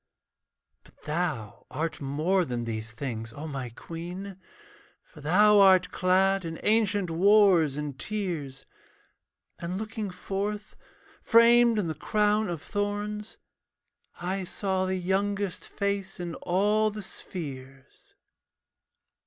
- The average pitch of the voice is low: No, medium, 185 Hz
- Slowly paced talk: Yes, slow, 115 wpm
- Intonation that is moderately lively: Yes, average, 4.7 semitones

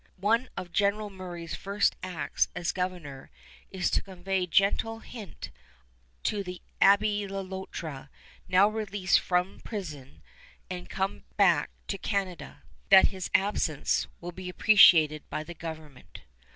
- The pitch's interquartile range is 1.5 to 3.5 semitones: Yes, average, 2.9 semitones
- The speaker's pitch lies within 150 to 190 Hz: Yes, medium, 185 Hz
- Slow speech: Yes, slow, 130 wpm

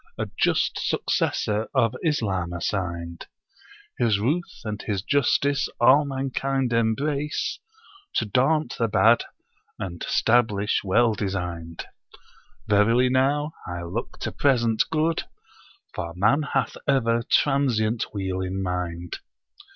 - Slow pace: Yes, slow, 110 wpm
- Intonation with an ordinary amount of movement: No, wide, 6.0 semitones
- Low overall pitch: Yes, low, 115 Hz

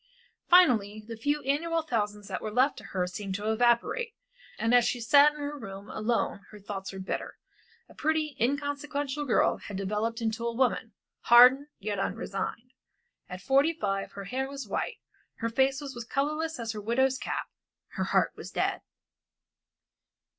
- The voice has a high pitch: Yes, high, 240 Hz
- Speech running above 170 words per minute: No, average, 165 wpm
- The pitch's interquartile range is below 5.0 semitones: No, average, 5.3 semitones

